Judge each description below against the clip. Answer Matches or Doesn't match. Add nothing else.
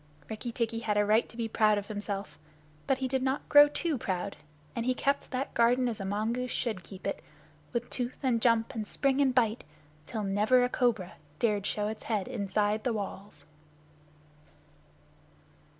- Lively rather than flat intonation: Doesn't match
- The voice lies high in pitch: Matches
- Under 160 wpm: Doesn't match